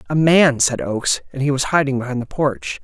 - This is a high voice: No, low, 130 Hz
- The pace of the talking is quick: Yes, fast, 235 wpm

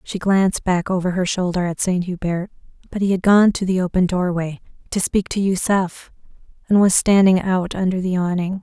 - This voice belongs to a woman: Yes, female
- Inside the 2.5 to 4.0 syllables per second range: No, 5.2 syllables/s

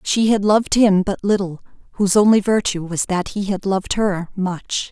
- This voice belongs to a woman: Yes, female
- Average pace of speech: Yes, average, 195 wpm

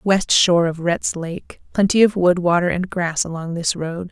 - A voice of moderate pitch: Yes, medium, 175 Hz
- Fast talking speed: No, average, 190 wpm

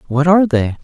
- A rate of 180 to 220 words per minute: Yes, fast, 215 wpm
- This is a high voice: No, medium, 155 Hz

